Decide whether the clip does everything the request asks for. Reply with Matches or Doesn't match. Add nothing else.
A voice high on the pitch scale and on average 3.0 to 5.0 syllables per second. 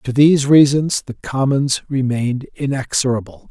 Doesn't match